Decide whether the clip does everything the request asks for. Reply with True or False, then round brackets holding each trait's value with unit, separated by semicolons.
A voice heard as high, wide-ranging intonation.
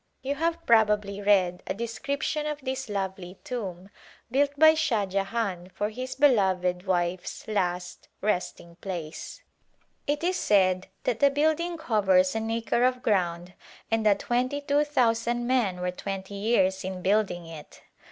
True (210 Hz; 5.8 semitones)